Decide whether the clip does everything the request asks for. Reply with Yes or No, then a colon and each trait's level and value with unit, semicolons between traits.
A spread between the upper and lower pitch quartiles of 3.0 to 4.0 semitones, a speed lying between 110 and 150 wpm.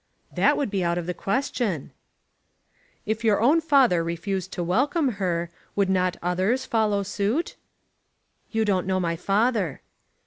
No: average, 4.6 semitones; average, 145 wpm